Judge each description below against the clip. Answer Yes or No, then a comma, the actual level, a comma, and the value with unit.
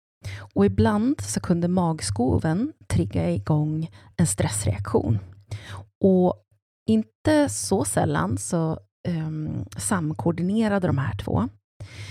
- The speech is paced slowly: Yes, slow, 95 wpm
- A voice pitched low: No, medium, 150 Hz